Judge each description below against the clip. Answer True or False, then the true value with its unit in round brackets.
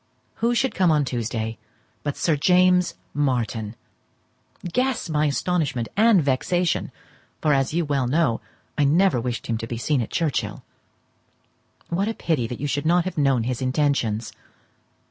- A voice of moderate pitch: True (145 Hz)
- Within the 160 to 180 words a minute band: False (150 wpm)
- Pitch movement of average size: False (6.0 semitones)